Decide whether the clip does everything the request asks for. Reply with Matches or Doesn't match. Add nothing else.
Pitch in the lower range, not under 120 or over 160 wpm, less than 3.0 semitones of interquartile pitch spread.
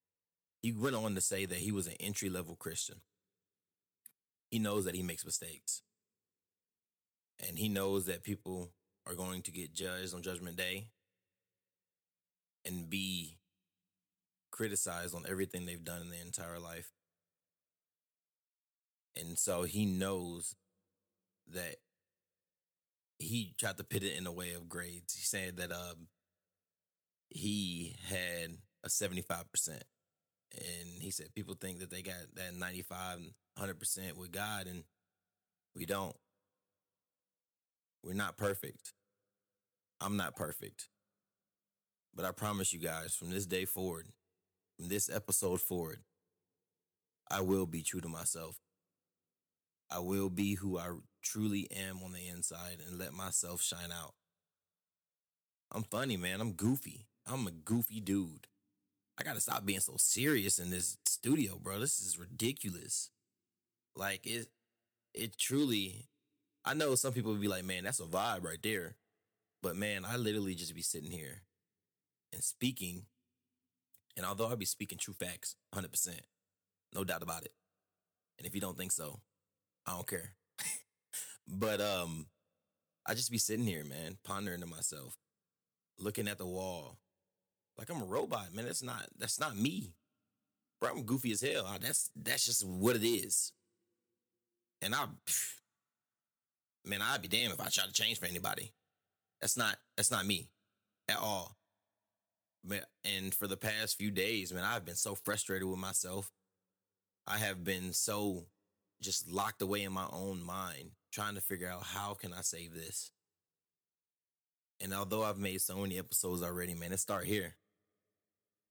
Matches